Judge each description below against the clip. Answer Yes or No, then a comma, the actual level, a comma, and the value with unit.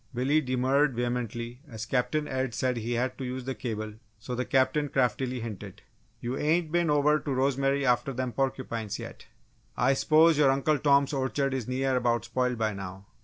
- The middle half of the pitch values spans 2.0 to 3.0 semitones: Yes, narrow, 2.5 semitones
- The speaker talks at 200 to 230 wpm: No, average, 180 wpm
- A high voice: No, low, 130 Hz